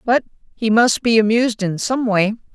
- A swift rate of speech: No, average, 190 wpm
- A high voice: Yes, high, 225 Hz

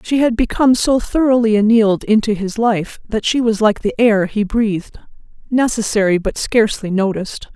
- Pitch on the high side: Yes, high, 220 Hz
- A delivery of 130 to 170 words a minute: Yes, average, 160 wpm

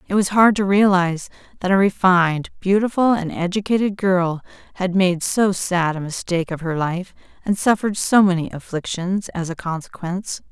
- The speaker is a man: No, female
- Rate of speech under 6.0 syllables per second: Yes, 5.2 syllables/s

